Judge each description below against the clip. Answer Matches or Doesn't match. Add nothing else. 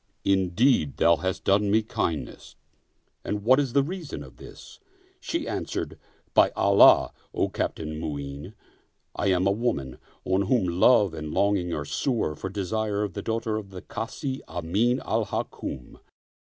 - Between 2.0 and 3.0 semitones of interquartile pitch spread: Doesn't match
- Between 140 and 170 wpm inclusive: Matches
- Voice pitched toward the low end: Matches